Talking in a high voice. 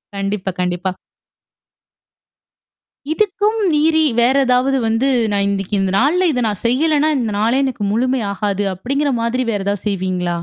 Yes: high, 235 Hz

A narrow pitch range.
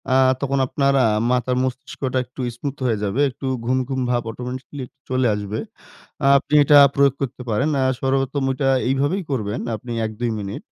Yes: narrow, 2.3 semitones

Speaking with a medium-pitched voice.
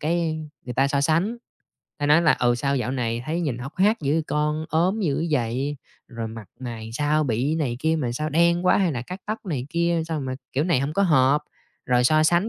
Yes: medium, 150 Hz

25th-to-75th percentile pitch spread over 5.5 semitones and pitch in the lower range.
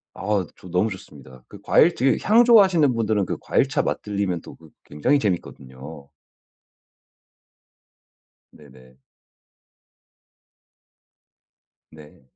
Yes: wide, 7.8 semitones; very low, 95 Hz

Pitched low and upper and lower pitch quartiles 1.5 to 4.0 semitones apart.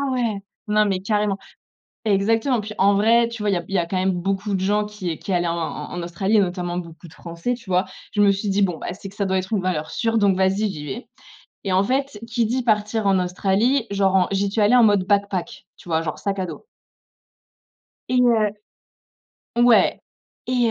No: high, 200 Hz; average, 2.8 semitones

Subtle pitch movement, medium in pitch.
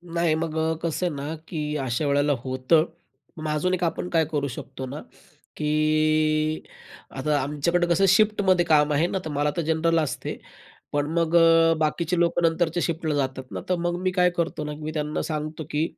Yes: narrow, 2.2 semitones; medium, 155 Hz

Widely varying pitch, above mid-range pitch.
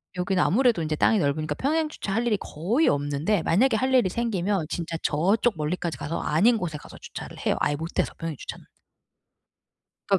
No: wide, 6.7 semitones; medium, 180 Hz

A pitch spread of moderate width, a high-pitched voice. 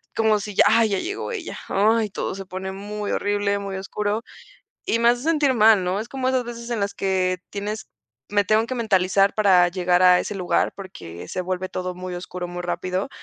Yes: average, 3.1 semitones; high, 200 Hz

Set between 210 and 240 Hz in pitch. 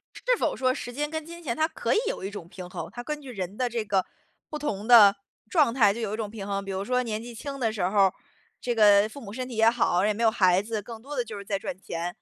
Yes: high, 225 Hz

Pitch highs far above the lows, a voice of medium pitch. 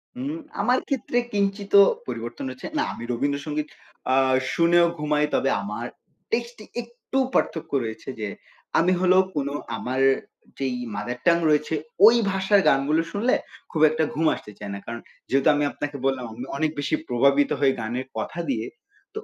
Yes: wide, 7.1 semitones; medium, 150 Hz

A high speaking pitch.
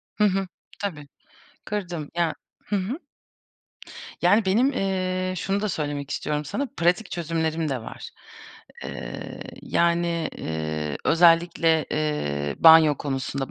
No: medium, 165 Hz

